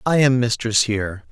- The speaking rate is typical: Yes, average, 185 wpm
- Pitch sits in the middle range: No, low, 120 Hz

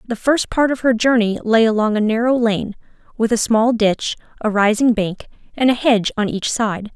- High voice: Yes, high, 225 Hz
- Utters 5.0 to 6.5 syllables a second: Yes, 5.1 syllables/s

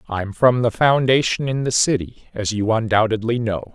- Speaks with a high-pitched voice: No, low, 115 Hz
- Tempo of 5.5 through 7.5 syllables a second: No, 4.9 syllables/s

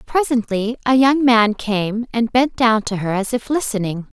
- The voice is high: Yes, high, 230 Hz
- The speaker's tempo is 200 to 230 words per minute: No, average, 185 wpm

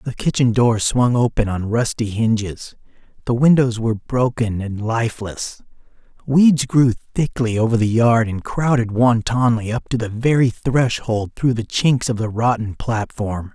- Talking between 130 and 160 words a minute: Yes, average, 155 wpm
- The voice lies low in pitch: Yes, low, 115 Hz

